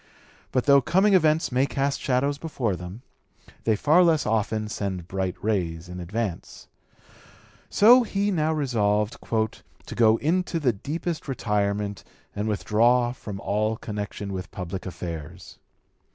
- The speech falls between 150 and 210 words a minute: No, slow, 135 wpm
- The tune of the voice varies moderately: No, wide, 6.2 semitones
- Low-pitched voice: Yes, low, 110 Hz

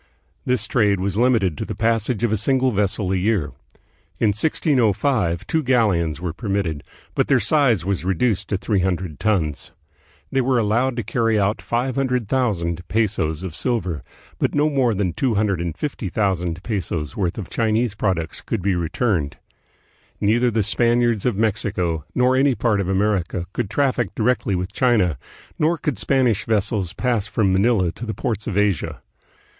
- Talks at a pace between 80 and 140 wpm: No, average, 160 wpm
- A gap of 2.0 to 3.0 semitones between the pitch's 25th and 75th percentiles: No, average, 4.5 semitones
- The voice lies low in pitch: Yes, low, 105 Hz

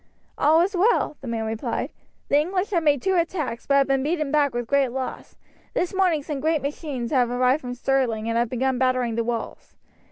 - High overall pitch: Yes, very high, 275 Hz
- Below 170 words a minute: No, average, 200 wpm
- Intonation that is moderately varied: Yes, average, 4.1 semitones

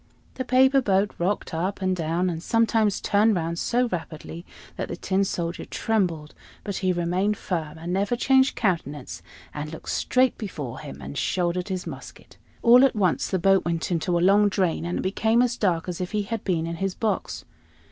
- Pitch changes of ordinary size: Yes, average, 3.9 semitones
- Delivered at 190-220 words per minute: Yes, average, 195 wpm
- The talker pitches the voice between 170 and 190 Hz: Yes, medium, 185 Hz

